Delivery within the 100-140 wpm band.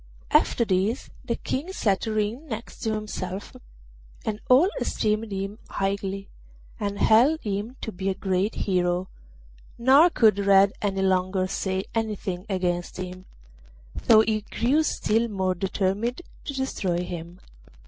Yes: slow, 135 wpm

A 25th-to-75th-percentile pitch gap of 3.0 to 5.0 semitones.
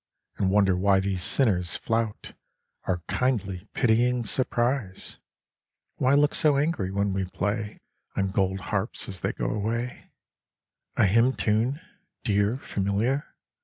Yes: average, 4.3 semitones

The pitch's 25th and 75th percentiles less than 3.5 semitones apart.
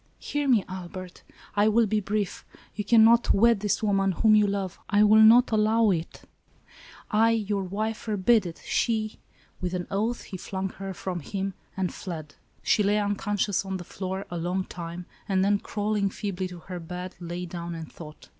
Yes: average, 2.8 semitones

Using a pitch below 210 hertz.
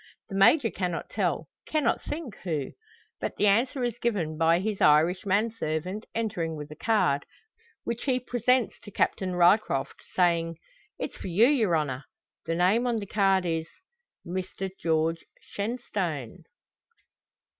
Yes: high, 190 Hz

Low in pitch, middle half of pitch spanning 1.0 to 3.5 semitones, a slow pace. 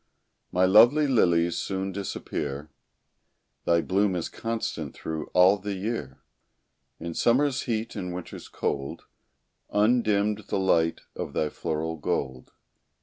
No: very low, 95 Hz; average, 4.7 semitones; slow, 120 wpm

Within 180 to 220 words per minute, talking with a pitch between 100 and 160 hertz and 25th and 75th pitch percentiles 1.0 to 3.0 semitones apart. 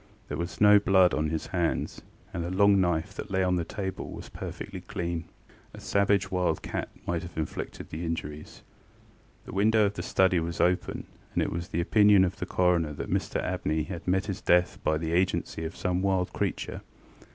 No: average, 195 wpm; very low, 90 Hz; narrow, 2.6 semitones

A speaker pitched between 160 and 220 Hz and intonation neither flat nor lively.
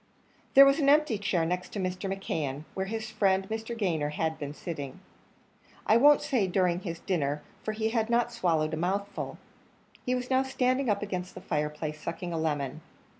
No: high, 190 Hz; wide, 5.8 semitones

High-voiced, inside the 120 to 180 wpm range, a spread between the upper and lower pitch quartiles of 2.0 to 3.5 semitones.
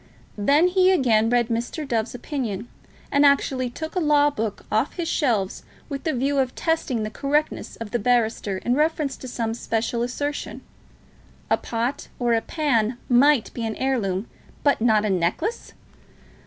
No: high, 245 Hz; average, 165 wpm; average, 4.3 semitones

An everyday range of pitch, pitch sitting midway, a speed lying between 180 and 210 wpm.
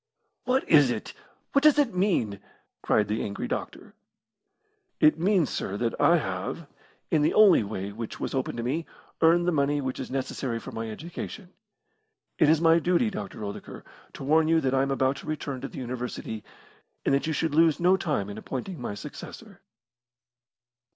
No: wide, 6.0 semitones; medium, 145 Hz; average, 185 wpm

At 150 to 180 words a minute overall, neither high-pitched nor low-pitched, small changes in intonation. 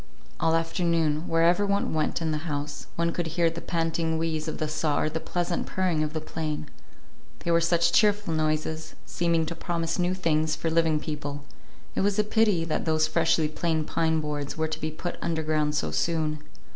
No: average, 195 wpm; medium, 160 Hz; narrow, 1.5 semitones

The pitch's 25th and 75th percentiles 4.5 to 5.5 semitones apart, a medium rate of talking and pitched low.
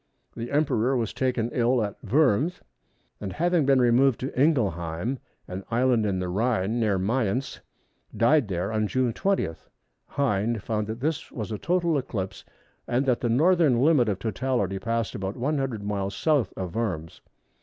Yes: average, 4.8 semitones; average, 160 wpm; low, 115 Hz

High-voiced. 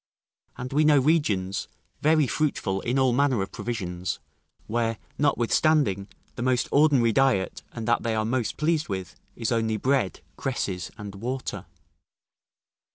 No: low, 120 Hz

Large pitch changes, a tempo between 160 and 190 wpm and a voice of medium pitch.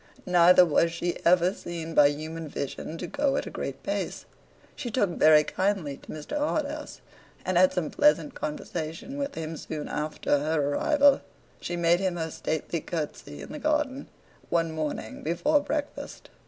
Yes: wide, 9.0 semitones; average, 165 wpm; medium, 170 Hz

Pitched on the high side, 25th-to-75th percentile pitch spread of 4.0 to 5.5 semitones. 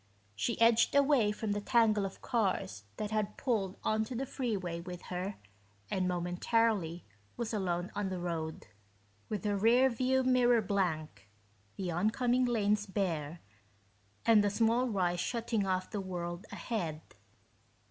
Yes: high, 205 Hz; average, 4.4 semitones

